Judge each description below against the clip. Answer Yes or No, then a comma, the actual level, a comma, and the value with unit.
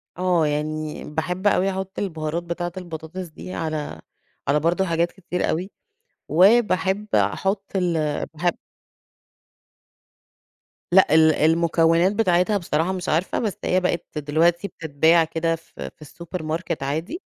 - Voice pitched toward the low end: No, medium, 170 Hz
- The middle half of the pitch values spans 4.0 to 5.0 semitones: No, average, 2.8 semitones